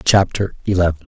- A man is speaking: Yes, male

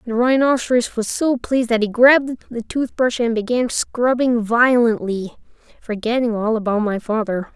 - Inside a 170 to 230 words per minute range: No, average, 150 wpm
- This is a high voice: Yes, high, 235 Hz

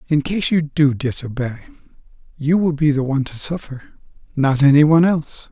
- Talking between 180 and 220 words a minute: No, average, 165 wpm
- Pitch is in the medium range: Yes, medium, 145 Hz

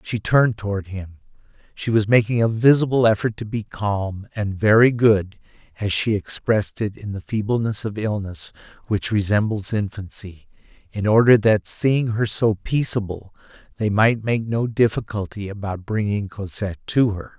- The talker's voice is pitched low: Yes, low, 105 Hz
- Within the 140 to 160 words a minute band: Yes, average, 155 wpm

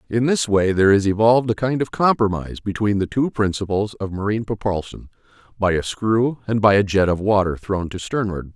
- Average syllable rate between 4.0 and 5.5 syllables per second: No, 5.7 syllables/s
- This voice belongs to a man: Yes, male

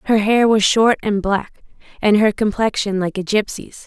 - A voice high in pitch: Yes, high, 210 Hz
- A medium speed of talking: Yes, average, 185 wpm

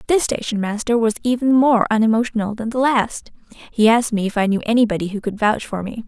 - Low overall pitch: No, high, 225 Hz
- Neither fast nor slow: No, fast, 215 wpm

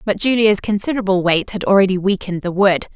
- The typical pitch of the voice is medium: No, high, 195 Hz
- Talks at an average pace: Yes, average, 185 wpm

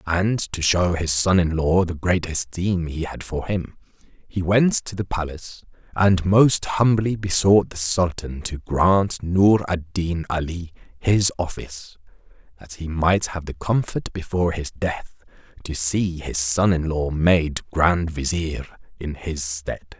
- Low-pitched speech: Yes, very low, 85 Hz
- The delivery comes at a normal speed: Yes, average, 160 wpm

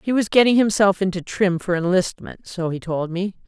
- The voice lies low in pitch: No, high, 190 Hz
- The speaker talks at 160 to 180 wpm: No, fast, 205 wpm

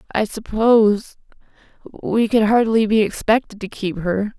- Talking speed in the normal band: No, slow, 125 wpm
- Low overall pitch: No, high, 215 Hz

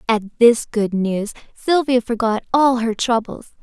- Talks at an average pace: Yes, average, 150 wpm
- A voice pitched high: Yes, high, 230 Hz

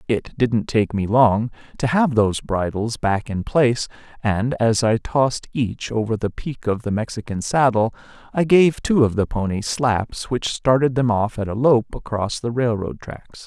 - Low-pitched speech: Yes, low, 115 Hz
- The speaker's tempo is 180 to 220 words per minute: Yes, average, 185 wpm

